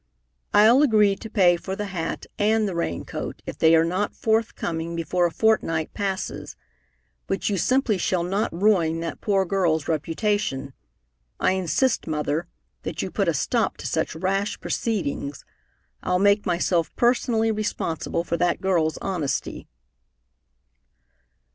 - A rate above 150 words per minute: No, average, 140 wpm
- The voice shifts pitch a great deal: No, average, 4.2 semitones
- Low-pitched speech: No, medium, 185 Hz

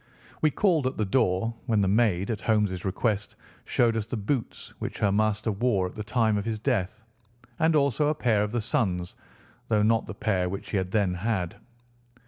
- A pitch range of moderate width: Yes, average, 3.2 semitones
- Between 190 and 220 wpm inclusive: Yes, average, 200 wpm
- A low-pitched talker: Yes, low, 110 Hz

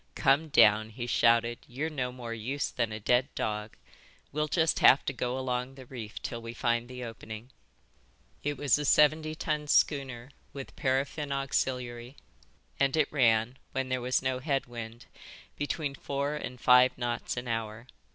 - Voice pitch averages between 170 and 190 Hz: No, low, 125 Hz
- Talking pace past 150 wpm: Yes, average, 165 wpm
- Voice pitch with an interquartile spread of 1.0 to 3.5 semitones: Yes, average, 2.9 semitones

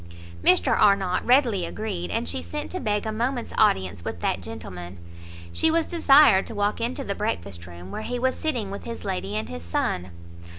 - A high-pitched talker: Yes, high, 200 Hz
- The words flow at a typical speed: Yes, average, 195 wpm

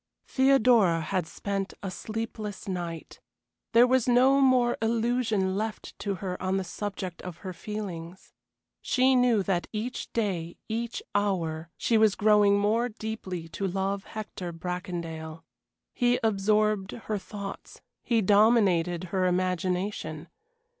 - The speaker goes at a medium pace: No, slow, 125 wpm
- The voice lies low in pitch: No, high, 200 Hz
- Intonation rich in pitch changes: No, average, 3.6 semitones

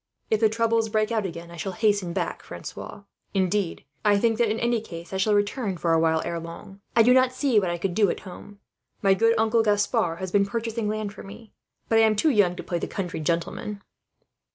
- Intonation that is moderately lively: Yes, average, 3.7 semitones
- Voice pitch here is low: No, high, 205 Hz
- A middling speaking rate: No, fast, 230 wpm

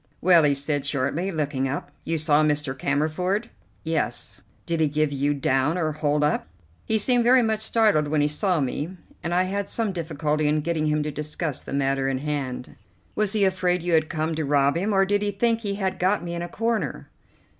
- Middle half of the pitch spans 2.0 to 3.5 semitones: No, average, 4.5 semitones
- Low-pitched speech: No, medium, 155 Hz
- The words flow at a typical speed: No, fast, 210 wpm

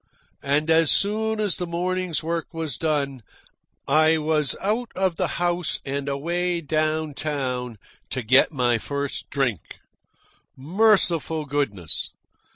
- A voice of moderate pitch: Yes, medium, 155 Hz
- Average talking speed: No, slow, 125 wpm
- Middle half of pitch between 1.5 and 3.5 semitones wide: No, average, 3.9 semitones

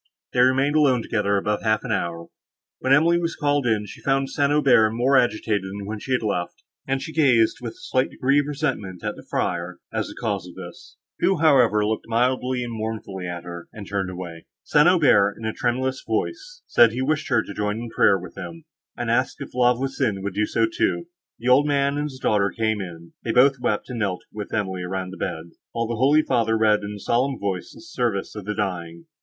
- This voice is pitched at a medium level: No, low, 115 Hz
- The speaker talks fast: Yes, fast, 225 wpm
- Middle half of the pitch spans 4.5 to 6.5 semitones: Yes, average, 4.8 semitones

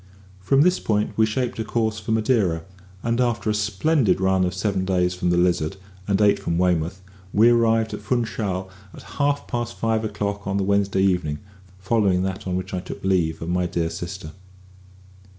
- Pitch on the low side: Yes, low, 100 Hz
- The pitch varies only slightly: No, average, 3.5 semitones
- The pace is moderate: Yes, average, 185 wpm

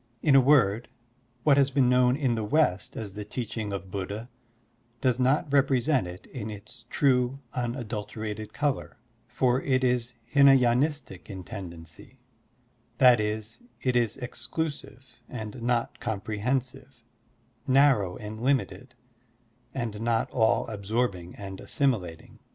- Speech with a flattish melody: No, average, 3.8 semitones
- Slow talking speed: Yes, slow, 130 wpm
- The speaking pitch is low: Yes, low, 120 Hz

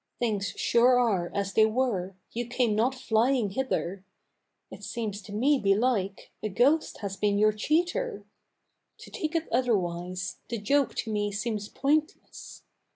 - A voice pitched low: No, high, 220 Hz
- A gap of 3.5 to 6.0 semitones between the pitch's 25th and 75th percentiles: Yes, average, 4.3 semitones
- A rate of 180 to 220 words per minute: No, average, 150 wpm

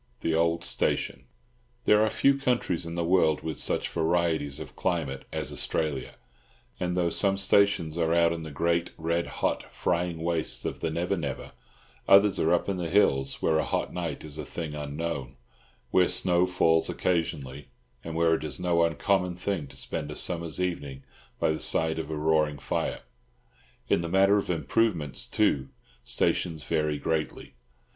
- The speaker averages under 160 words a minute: No, average, 170 wpm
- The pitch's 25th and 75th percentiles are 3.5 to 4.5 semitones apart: No, narrow, 2.4 semitones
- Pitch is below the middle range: Yes, very low, 85 Hz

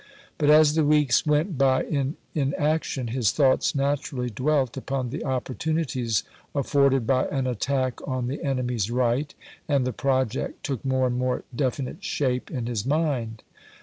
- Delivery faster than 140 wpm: Yes, average, 150 wpm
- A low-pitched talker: Yes, low, 130 Hz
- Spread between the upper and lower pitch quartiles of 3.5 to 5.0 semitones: No, narrow, 2.5 semitones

